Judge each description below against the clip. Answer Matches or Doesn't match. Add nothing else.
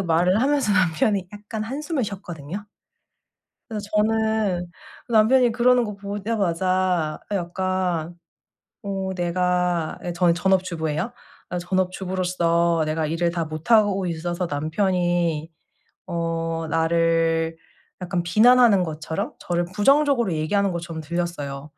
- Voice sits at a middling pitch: Matches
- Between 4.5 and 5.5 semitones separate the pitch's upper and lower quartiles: Doesn't match